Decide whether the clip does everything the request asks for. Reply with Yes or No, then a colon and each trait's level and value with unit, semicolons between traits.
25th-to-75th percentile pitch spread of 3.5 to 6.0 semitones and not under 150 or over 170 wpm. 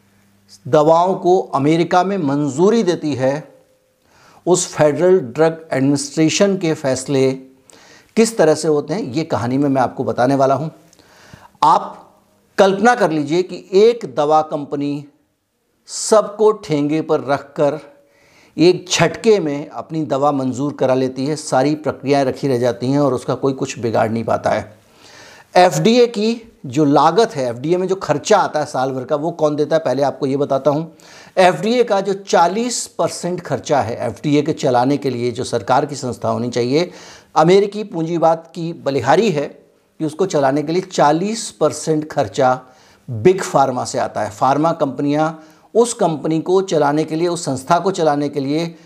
Yes: average, 4.2 semitones; average, 165 wpm